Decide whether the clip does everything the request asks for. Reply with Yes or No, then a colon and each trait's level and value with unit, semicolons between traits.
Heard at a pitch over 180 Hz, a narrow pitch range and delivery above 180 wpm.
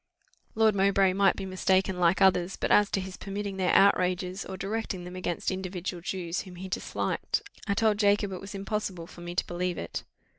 Yes: high, 190 Hz; narrow, 1.7 semitones; average, 195 wpm